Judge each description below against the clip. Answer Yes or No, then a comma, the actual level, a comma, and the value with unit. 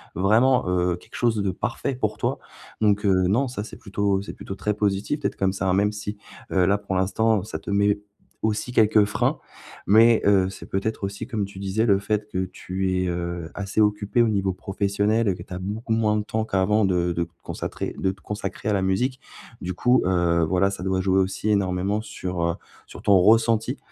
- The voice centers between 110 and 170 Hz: No, low, 100 Hz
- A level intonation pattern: Yes, narrow, 2.3 semitones